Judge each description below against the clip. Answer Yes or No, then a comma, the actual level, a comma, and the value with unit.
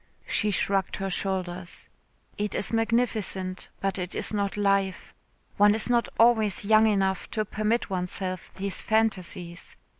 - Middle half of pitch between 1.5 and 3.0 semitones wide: Yes, narrow, 2.4 semitones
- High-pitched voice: Yes, high, 200 Hz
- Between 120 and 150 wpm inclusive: Yes, average, 140 wpm